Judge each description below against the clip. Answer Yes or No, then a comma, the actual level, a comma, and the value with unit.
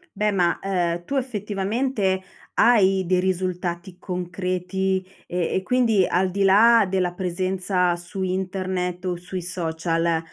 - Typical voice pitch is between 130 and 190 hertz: Yes, medium, 185 Hz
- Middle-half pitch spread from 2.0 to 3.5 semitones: No, narrow, 1.5 semitones